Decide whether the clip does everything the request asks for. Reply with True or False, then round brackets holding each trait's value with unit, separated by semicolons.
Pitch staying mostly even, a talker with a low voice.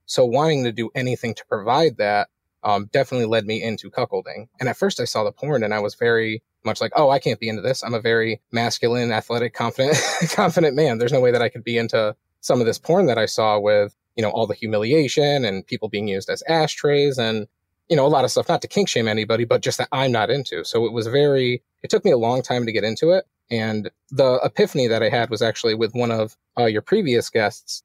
True (2.3 semitones; 115 Hz)